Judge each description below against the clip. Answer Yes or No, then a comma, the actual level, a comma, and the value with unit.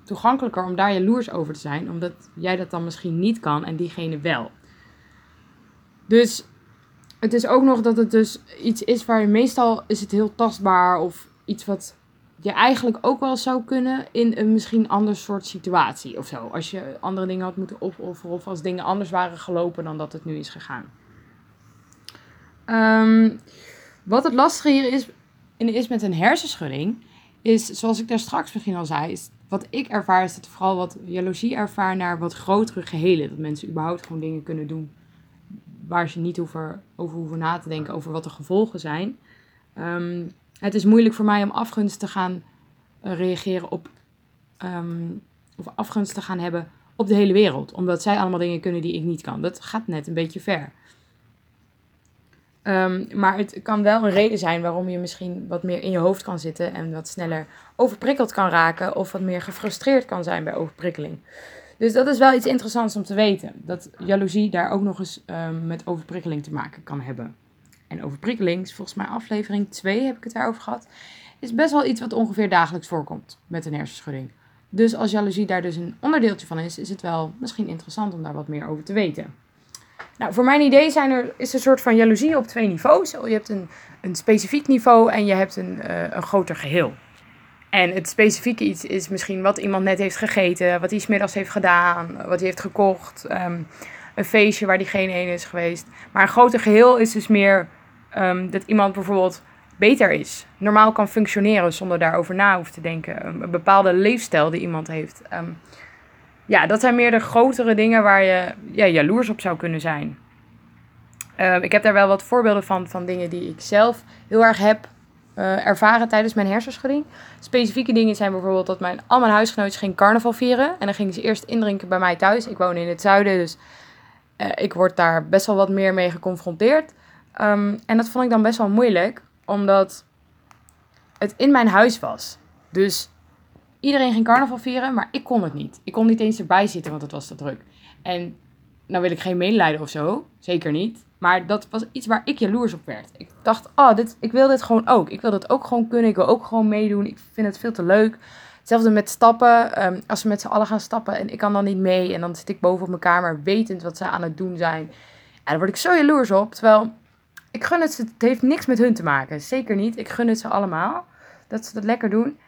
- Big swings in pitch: No, average, 4.3 semitones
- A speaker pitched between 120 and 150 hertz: No, high, 195 Hz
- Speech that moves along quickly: Yes, fast, 210 wpm